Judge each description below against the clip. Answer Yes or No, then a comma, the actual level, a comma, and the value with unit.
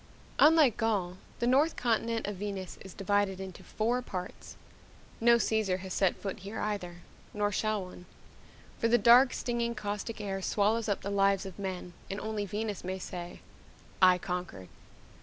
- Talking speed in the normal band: Yes, average, 160 wpm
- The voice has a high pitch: Yes, high, 205 Hz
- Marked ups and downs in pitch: No, average, 3.2 semitones